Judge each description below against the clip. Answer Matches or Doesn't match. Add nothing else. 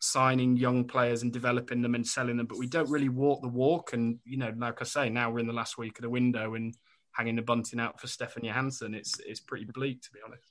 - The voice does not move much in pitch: Matches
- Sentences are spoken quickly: Matches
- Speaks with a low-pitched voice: Matches